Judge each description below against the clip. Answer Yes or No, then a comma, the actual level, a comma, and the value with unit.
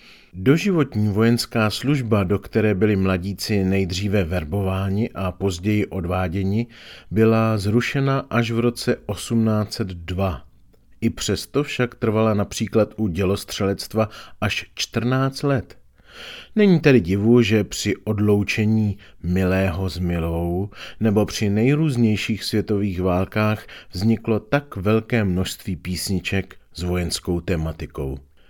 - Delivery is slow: Yes, slow, 105 wpm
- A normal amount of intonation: Yes, average, 3.2 semitones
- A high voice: No, low, 105 Hz